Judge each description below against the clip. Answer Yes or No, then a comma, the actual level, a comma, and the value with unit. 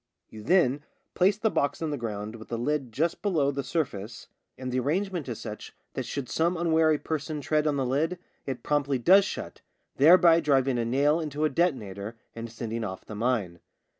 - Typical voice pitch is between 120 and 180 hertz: Yes, medium, 140 Hz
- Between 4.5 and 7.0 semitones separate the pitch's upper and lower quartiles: Yes, wide, 5.4 semitones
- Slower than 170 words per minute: No, average, 195 wpm